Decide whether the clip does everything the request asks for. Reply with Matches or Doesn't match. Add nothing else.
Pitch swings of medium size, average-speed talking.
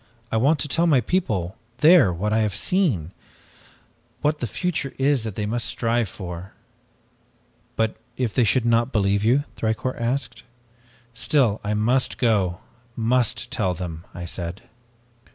Matches